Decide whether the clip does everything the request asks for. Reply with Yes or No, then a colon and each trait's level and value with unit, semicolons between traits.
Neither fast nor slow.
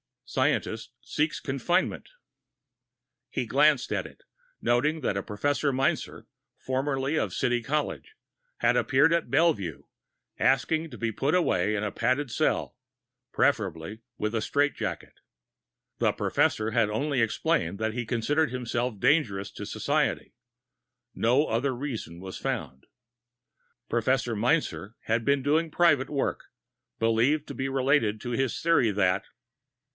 No: slow, 130 wpm